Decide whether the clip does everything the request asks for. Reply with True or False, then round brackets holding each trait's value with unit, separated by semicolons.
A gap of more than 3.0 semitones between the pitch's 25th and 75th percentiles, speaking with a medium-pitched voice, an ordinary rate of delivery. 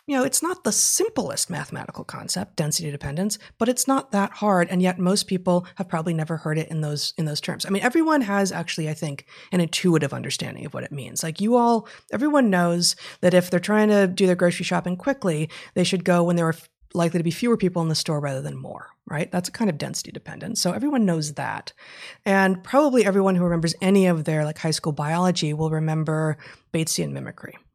False (3.9 semitones; 175 Hz; 220 wpm)